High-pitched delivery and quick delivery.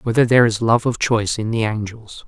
No: low, 115 Hz; fast, 235 wpm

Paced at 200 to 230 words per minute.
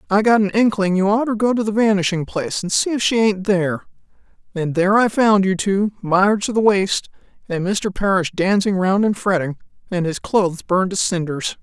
Yes: fast, 205 wpm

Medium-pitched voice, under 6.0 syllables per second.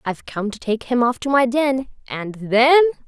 No: very high, 250 Hz; 5.0 syllables/s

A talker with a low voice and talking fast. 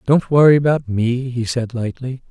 No: low, 125 Hz; average, 180 wpm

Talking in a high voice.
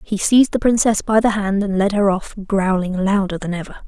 Yes: high, 200 Hz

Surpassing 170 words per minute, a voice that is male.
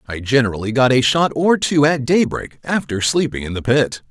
Yes: fast, 205 wpm; male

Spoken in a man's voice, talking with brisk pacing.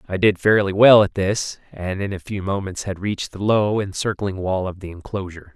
Yes: male; fast, 215 wpm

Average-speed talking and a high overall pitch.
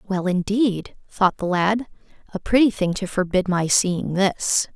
Yes: average, 165 wpm; high, 195 Hz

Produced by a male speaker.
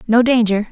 No: female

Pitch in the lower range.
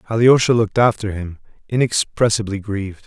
Yes: low, 105 Hz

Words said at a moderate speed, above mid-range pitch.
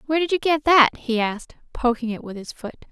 No: fast, 245 wpm; very high, 260 Hz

